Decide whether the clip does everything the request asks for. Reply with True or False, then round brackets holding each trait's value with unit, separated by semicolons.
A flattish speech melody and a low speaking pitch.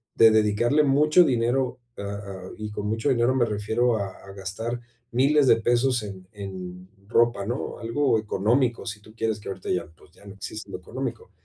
False (3.2 semitones; 110 Hz)